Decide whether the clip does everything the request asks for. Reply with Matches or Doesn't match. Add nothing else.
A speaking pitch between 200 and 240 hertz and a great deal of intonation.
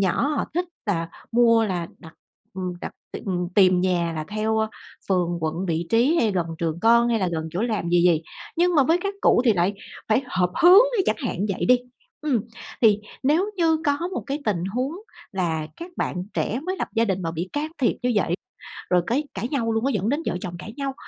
Matches